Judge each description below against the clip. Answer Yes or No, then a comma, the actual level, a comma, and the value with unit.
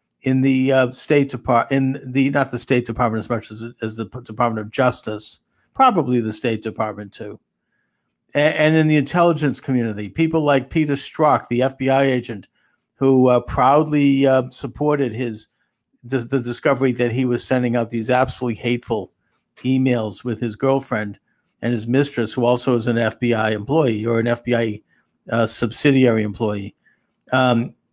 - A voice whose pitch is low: Yes, low, 125 Hz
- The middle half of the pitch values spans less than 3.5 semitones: Yes, narrow, 2.6 semitones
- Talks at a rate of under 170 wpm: Yes, average, 155 wpm